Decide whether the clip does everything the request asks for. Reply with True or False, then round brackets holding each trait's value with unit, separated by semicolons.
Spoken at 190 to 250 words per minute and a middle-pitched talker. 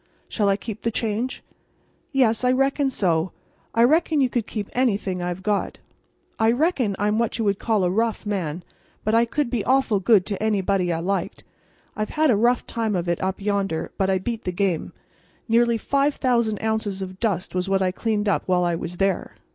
False (200 wpm; 210 Hz)